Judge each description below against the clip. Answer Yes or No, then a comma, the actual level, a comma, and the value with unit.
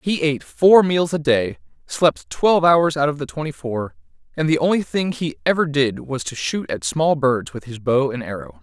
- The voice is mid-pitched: Yes, medium, 150 Hz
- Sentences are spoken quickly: Yes, fast, 225 wpm